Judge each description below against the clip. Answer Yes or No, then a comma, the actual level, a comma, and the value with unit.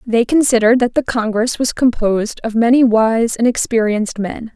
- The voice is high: Yes, high, 230 Hz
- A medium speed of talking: Yes, average, 170 wpm